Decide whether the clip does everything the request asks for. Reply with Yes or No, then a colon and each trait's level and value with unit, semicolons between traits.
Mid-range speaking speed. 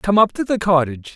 No: fast, 260 wpm